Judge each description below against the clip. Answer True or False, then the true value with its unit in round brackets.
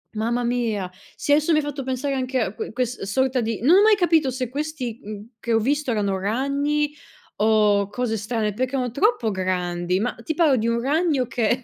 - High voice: True (245 Hz)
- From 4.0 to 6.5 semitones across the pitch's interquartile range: True (4.7 semitones)